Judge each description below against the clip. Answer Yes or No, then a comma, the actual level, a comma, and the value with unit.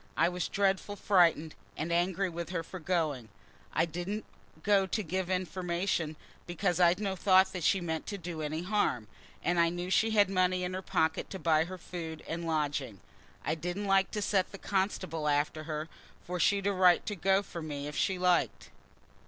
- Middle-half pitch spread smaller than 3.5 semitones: Yes, average, 2.9 semitones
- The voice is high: No, medium, 180 Hz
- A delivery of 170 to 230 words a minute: Yes, average, 190 wpm